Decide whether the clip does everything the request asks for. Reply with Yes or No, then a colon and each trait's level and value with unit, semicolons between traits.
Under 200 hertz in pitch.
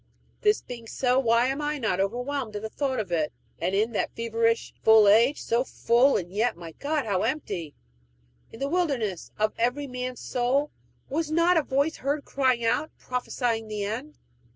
No: high, 245 Hz